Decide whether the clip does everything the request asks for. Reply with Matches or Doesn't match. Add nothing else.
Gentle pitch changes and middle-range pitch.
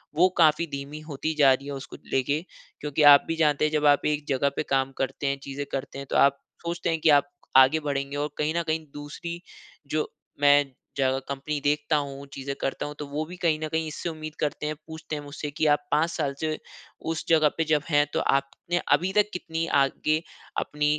Matches